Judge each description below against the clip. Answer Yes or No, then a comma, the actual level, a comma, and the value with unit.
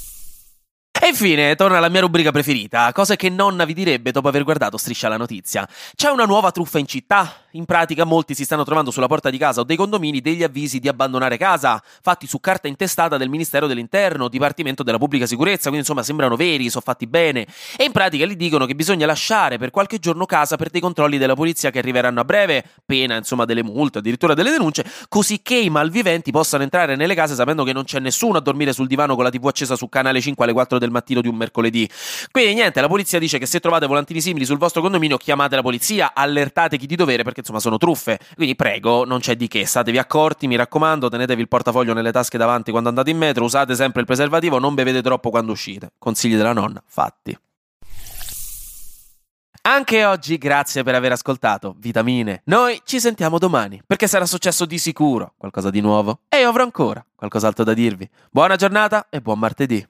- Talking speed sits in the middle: No, fast, 205 wpm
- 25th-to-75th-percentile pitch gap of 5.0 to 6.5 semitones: Yes, wide, 5.5 semitones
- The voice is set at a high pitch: No, medium, 140 Hz